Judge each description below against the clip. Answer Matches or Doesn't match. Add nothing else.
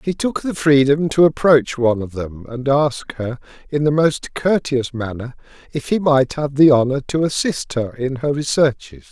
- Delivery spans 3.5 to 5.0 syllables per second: Matches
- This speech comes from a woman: Doesn't match